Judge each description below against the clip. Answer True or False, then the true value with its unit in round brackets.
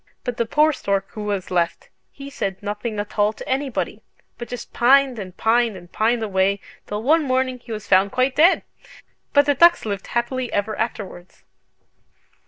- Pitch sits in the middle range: False (225 Hz)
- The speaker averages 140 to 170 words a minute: False (180 wpm)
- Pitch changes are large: False (4.3 semitones)